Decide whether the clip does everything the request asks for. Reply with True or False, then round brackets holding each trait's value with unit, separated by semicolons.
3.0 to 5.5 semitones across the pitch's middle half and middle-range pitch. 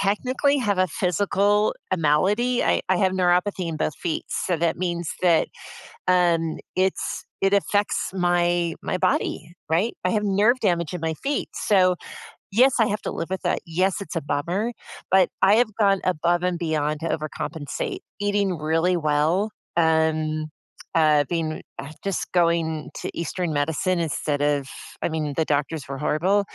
True (3.6 semitones; 175 Hz)